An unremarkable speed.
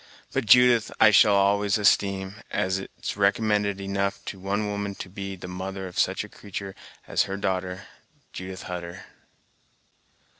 Yes: average, 150 wpm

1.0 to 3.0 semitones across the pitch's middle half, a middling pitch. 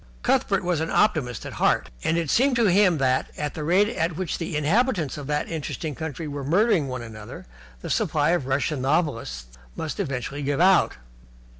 No: average, 4.4 semitones; medium, 150 Hz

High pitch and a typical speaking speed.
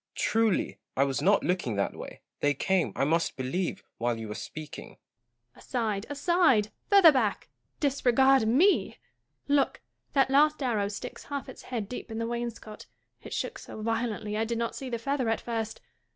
Yes: high, 225 Hz; average, 180 wpm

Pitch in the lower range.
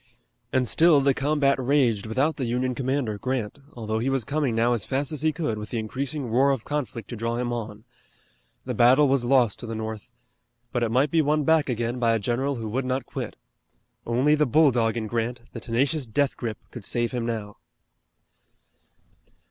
Yes: low, 125 Hz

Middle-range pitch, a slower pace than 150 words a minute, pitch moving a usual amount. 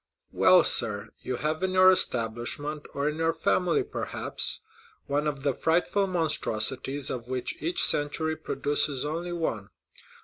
Yes: medium, 150 Hz; average, 140 wpm; average, 4.3 semitones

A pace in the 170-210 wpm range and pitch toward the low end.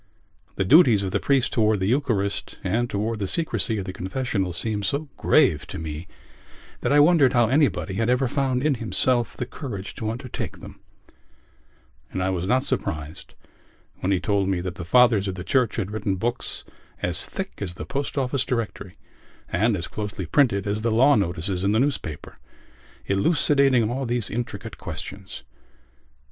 Yes: average, 175 wpm; low, 110 Hz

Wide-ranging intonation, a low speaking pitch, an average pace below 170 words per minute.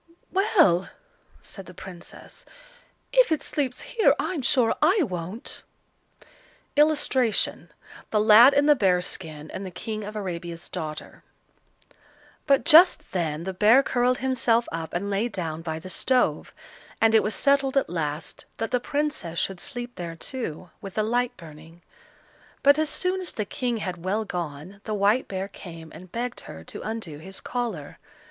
No: wide, 6.6 semitones; high, 210 Hz; average, 160 wpm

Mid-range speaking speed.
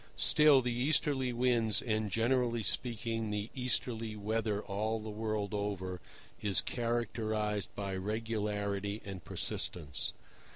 No: slow, 115 wpm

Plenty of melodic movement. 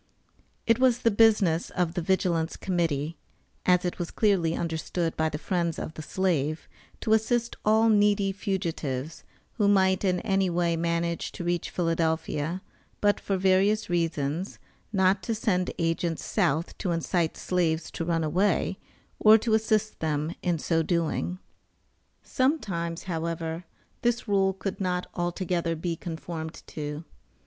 No: average, 3.1 semitones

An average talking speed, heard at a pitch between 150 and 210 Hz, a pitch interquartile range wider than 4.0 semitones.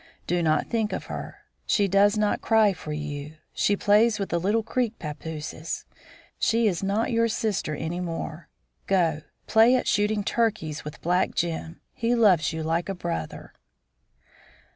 Yes: average, 155 wpm; high, 190 Hz; average, 5.2 semitones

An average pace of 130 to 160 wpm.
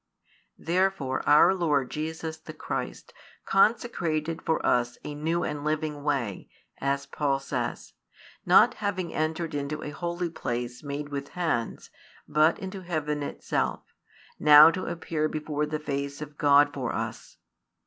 Yes: average, 140 wpm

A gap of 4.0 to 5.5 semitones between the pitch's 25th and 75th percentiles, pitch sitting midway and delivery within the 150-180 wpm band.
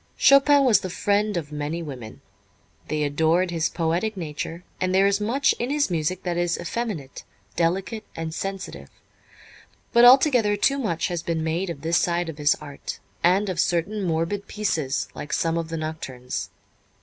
Yes: average, 4.4 semitones; medium, 170 Hz; average, 170 wpm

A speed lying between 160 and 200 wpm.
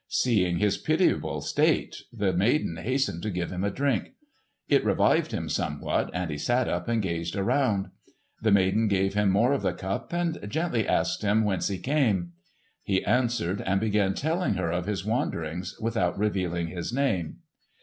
Yes: average, 170 wpm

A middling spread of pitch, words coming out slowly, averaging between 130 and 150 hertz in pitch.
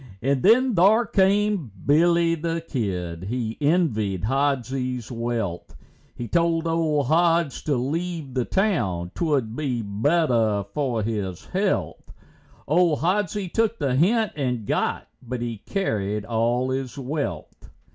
No: wide, 6.6 semitones; slow, 125 wpm; medium, 140 Hz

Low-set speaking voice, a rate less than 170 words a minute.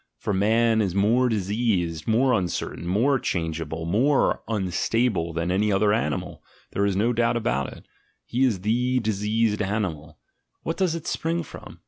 Yes: low, 105 Hz; average, 160 wpm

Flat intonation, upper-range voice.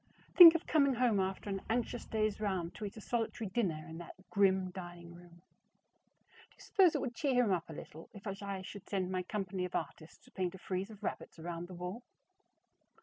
No: average, 3.6 semitones; high, 195 Hz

